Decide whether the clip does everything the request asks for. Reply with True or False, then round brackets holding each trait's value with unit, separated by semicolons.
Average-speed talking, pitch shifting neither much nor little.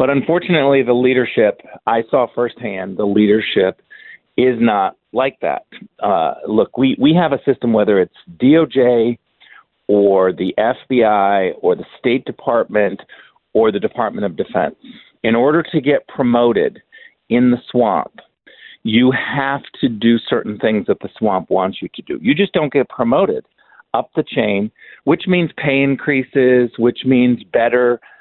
True (150 wpm; 3.4 semitones)